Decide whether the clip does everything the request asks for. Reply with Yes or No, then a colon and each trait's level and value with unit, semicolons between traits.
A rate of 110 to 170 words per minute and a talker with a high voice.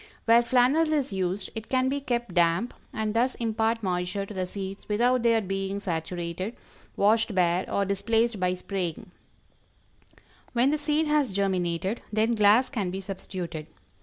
Yes: average, 155 wpm; high, 205 Hz